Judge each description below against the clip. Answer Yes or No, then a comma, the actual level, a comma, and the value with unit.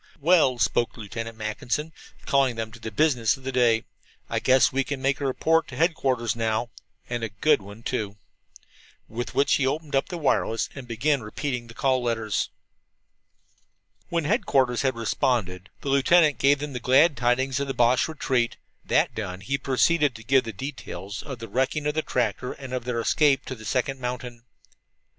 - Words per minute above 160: Yes, average, 185 wpm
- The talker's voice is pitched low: Yes, low, 130 Hz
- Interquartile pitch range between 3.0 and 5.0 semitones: Yes, average, 3.4 semitones